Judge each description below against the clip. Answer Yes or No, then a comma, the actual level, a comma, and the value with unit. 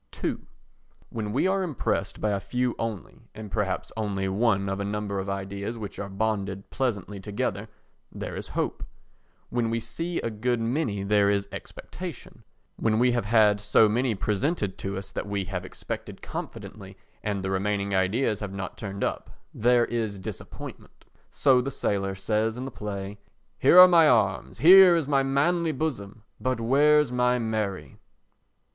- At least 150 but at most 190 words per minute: Yes, average, 165 wpm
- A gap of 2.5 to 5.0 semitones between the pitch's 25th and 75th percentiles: Yes, average, 3.9 semitones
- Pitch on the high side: No, low, 110 Hz